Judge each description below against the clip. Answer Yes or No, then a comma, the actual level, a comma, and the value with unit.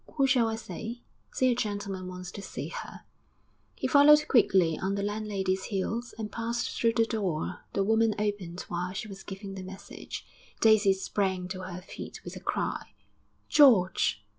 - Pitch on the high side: Yes, high, 205 Hz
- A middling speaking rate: Yes, average, 170 wpm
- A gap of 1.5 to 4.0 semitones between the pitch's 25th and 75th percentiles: Yes, average, 3.3 semitones